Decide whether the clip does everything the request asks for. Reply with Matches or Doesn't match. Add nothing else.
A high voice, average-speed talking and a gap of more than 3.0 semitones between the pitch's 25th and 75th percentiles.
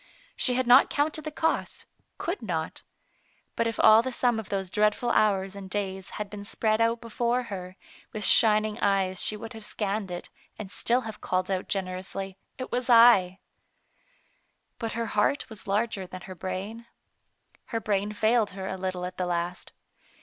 Matches